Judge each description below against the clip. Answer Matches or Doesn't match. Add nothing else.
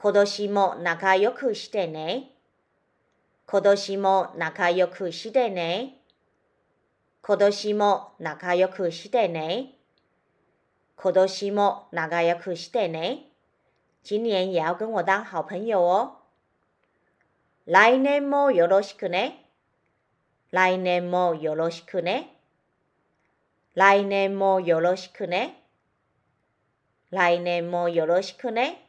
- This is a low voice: Doesn't match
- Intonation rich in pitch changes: Doesn't match